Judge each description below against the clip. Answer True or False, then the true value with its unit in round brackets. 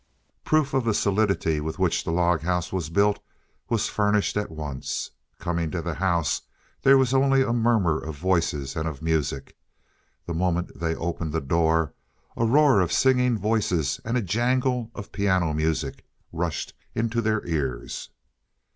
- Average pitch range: False (5.8 semitones)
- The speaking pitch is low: True (90 Hz)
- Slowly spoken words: False (160 wpm)